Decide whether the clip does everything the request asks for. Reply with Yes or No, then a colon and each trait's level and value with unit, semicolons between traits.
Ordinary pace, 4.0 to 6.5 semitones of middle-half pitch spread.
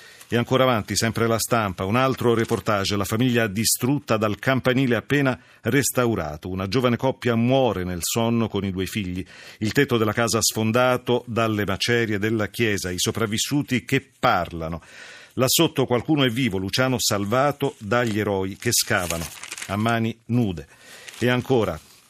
No: average, 150 wpm; average, 3.4 semitones